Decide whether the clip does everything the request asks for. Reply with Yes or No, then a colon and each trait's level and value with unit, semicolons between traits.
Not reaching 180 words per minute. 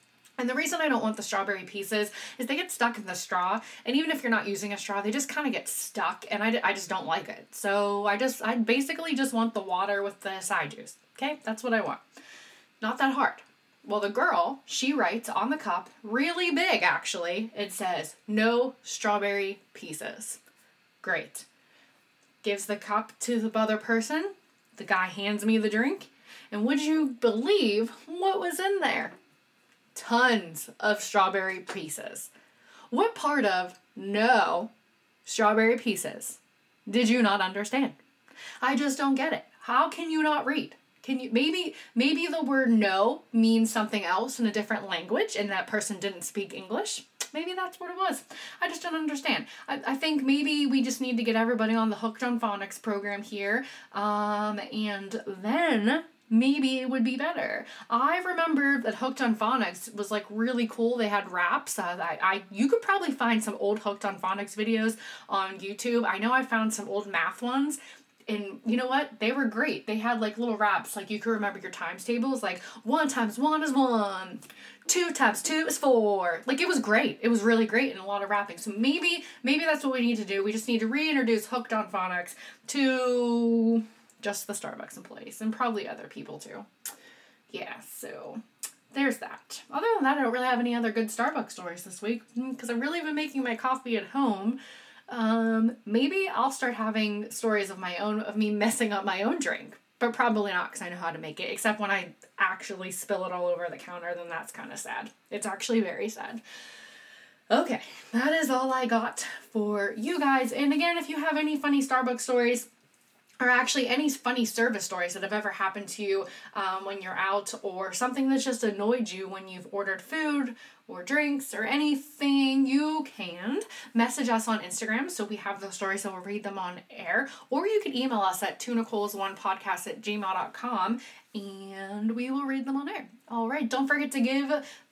No: average, 195 wpm